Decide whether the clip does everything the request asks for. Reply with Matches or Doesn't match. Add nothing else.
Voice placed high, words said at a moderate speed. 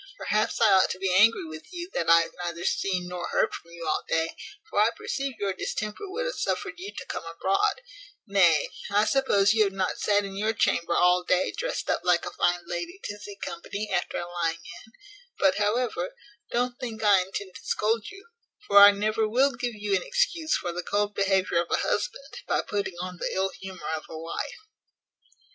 Doesn't match